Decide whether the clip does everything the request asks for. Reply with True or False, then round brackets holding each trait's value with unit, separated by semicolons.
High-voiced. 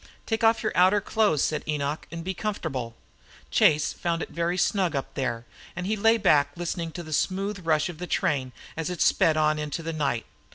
False (165 Hz)